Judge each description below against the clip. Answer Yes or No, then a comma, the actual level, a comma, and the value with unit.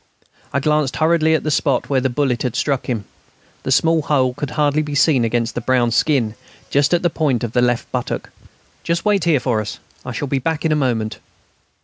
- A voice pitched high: No, medium, 140 Hz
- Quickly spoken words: Yes, fast, 220 wpm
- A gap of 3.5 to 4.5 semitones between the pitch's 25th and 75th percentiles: Yes, average, 3.8 semitones